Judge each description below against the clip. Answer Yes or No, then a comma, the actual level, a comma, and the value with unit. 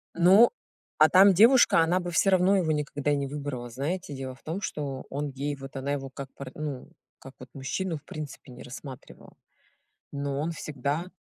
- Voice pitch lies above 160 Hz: No, medium, 145 Hz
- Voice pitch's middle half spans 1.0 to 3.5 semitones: No, average, 4.0 semitones